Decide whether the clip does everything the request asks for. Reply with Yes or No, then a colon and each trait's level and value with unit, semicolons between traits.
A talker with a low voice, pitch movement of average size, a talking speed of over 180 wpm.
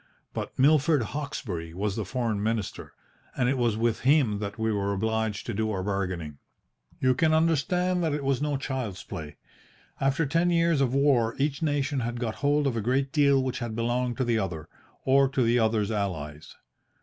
Yes: low, 120 Hz; average, 4.9 semitones; average, 190 wpm